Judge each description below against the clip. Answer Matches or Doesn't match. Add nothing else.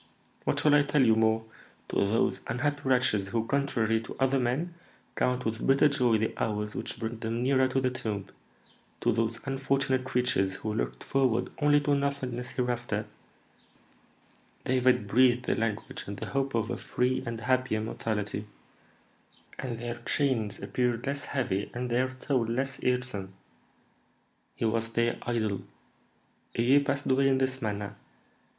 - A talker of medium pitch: Doesn't match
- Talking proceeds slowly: Doesn't match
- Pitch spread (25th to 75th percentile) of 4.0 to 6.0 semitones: Doesn't match